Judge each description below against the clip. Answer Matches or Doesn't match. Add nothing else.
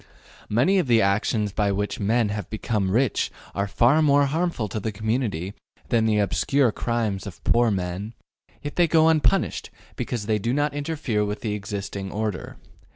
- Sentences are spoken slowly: Doesn't match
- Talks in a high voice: Doesn't match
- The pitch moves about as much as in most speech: Matches